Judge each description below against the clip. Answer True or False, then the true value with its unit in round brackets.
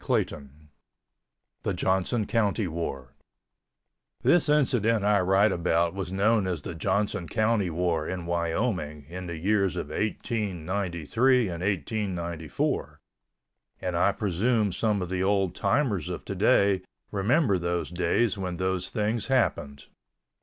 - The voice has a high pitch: False (95 Hz)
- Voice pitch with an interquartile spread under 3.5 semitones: False (3.8 semitones)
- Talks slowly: True (130 wpm)